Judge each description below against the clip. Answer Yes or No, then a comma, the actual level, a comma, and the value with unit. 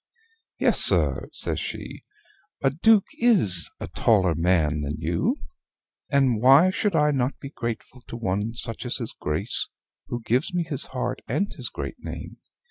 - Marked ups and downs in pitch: Yes, wide, 7.6 semitones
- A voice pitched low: Yes, low, 125 Hz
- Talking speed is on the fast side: No, average, 160 wpm